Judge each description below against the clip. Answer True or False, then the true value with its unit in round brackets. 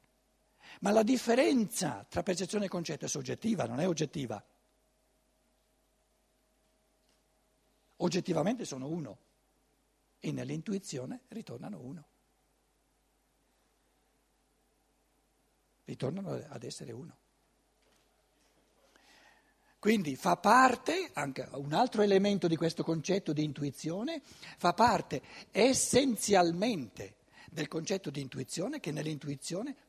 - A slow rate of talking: True (90 wpm)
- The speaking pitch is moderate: True (180 Hz)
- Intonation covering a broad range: True (6.9 semitones)